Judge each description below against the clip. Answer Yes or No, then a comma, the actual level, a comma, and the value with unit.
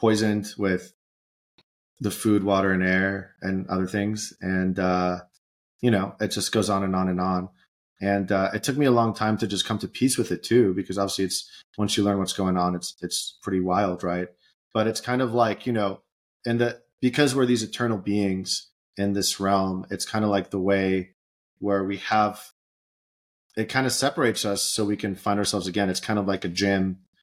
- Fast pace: Yes, fast, 210 wpm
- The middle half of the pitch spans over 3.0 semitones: No, narrow, 2.5 semitones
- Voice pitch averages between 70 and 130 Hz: Yes, low, 100 Hz